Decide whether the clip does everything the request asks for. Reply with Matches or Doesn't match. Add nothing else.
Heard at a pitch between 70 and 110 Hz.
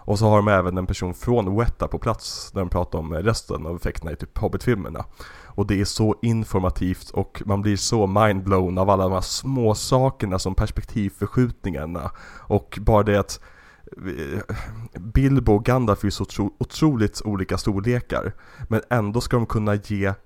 Matches